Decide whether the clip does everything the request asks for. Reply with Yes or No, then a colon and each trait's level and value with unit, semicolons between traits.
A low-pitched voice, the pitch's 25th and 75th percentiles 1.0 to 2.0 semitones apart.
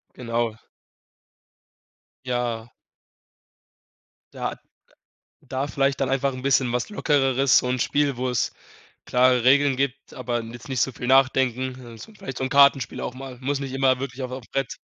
Yes: low, 130 Hz; narrow, 1.7 semitones